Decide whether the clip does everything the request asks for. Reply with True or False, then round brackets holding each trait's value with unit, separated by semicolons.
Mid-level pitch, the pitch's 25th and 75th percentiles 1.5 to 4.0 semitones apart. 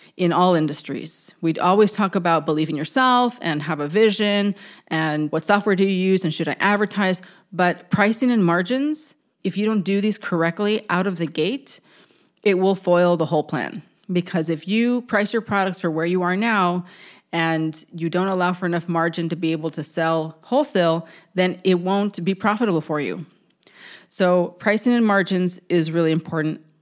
True (180 Hz; 3.6 semitones)